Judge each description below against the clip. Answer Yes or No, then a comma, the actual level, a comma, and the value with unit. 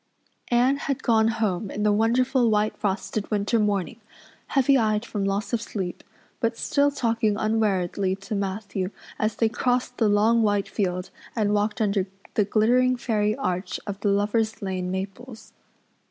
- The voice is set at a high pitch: Yes, high, 215 Hz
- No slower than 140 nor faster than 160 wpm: Yes, average, 155 wpm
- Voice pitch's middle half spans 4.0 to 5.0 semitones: No, narrow, 2.5 semitones